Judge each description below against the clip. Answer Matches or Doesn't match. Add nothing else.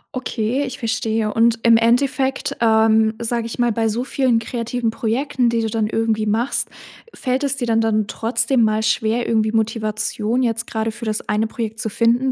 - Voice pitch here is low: Doesn't match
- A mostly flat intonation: Matches